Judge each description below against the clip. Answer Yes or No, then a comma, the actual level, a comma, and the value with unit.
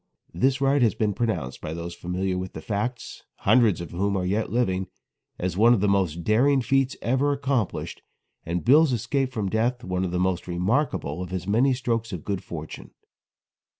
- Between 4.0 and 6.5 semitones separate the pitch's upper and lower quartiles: Yes, wide, 5.5 semitones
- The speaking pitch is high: No, low, 105 Hz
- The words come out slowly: No, average, 185 wpm